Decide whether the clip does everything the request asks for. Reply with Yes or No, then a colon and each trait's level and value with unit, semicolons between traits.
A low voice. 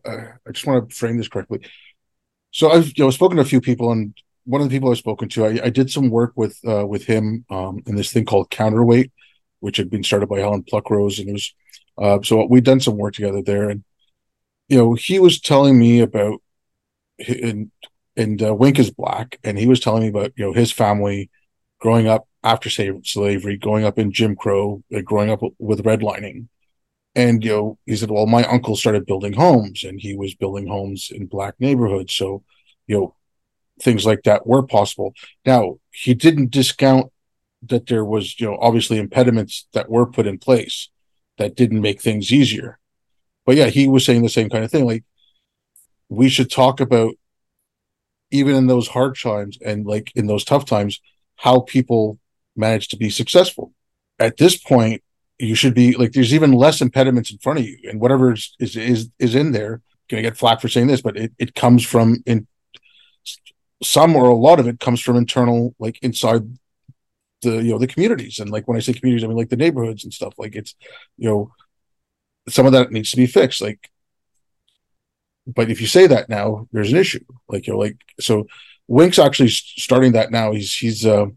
Yes: low, 115 Hz